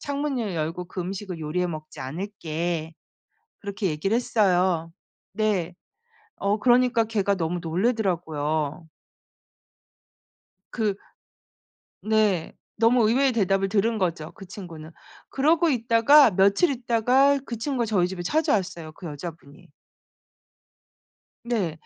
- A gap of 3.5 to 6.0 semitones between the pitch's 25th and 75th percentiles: Yes, average, 5.3 semitones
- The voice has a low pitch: No, high, 195 Hz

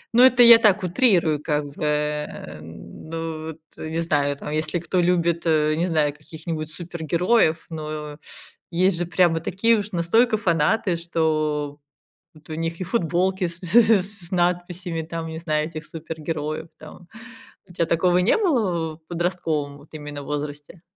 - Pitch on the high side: No, medium, 165 Hz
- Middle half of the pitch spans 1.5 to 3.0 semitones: Yes, average, 2.7 semitones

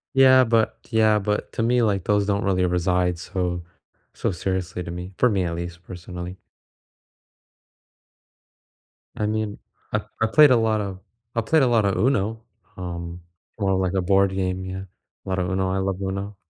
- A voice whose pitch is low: Yes, very low, 95 Hz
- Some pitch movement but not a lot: Yes, average, 3.2 semitones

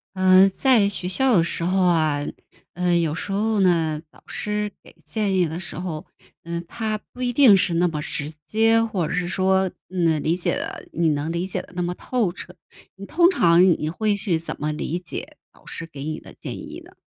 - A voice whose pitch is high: No, medium, 180 Hz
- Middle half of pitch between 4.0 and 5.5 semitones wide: No, average, 3.5 semitones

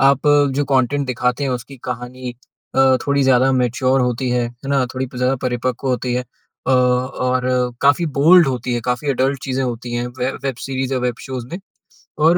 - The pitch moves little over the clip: Yes, narrow, 1.5 semitones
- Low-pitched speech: Yes, low, 130 Hz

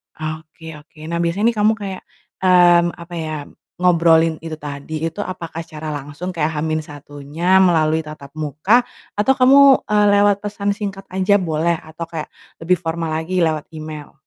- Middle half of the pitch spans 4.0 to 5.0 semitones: No, average, 3.2 semitones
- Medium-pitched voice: Yes, medium, 165 Hz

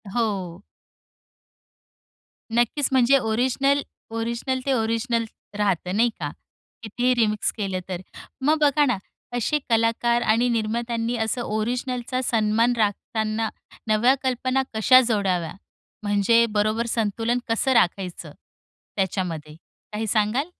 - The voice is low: No, high, 230 Hz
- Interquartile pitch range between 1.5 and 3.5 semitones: Yes, average, 2.8 semitones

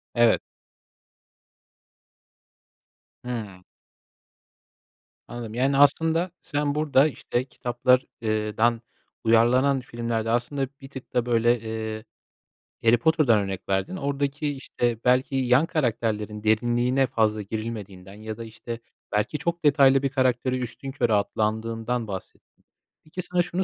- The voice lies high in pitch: No, low, 120 Hz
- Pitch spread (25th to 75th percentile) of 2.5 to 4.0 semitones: Yes, average, 3.7 semitones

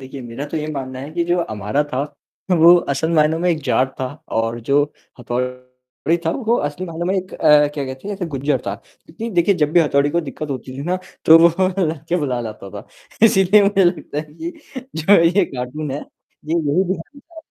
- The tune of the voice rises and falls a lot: No, average, 4.8 semitones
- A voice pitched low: No, medium, 155 Hz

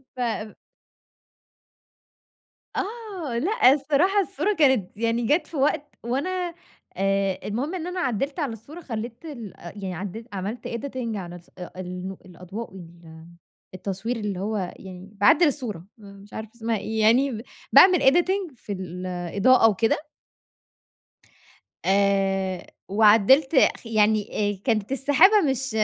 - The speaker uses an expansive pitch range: Yes, wide, 6.2 semitones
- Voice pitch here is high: Yes, high, 225 Hz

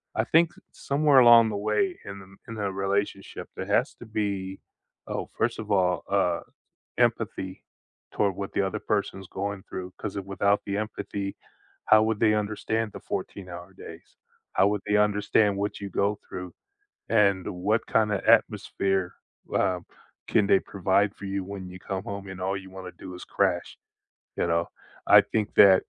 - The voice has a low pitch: Yes, low, 100 Hz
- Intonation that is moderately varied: No, narrow, 1.8 semitones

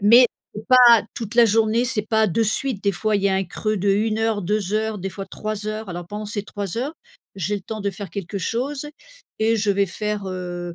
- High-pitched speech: Yes, high, 210 Hz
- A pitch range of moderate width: No, narrow, 2.2 semitones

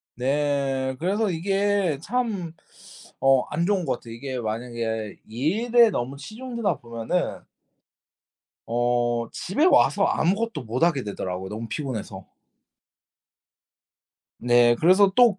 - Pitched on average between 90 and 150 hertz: Yes, medium, 140 Hz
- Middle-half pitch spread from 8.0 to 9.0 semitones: Yes, wide, 8.7 semitones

